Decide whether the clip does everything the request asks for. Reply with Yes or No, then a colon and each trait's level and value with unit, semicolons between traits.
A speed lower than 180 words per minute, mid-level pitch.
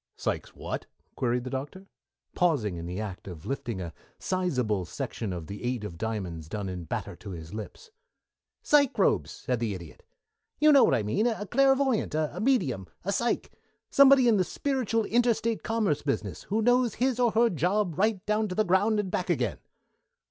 No: average, 185 wpm; medium, 180 Hz